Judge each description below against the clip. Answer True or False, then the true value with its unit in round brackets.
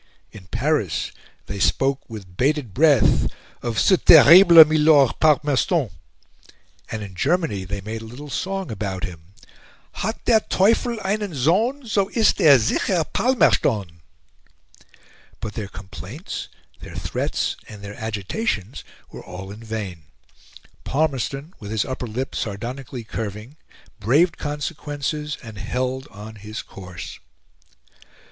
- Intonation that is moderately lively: False (7.4 semitones)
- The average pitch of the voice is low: True (125 Hz)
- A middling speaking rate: False (125 wpm)